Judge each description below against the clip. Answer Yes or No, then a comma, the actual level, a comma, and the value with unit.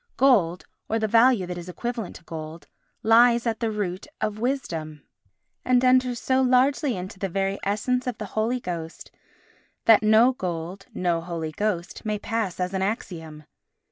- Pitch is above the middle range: Yes, high, 210 Hz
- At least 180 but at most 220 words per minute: No, average, 165 wpm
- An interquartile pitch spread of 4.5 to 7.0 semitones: Yes, average, 5.2 semitones